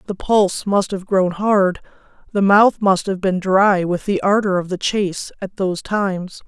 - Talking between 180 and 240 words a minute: Yes, average, 195 wpm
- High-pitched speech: Yes, high, 195 Hz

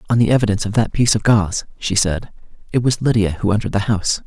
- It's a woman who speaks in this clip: No, male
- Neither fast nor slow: No, fast, 240 wpm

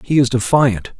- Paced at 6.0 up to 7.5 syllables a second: No, 4.6 syllables/s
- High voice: No, low, 125 Hz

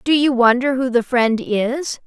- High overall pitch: Yes, very high, 255 Hz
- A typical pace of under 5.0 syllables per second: Yes, 4.0 syllables/s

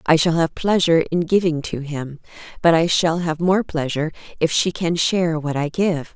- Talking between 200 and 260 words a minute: Yes, fast, 205 wpm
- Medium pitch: Yes, medium, 165 Hz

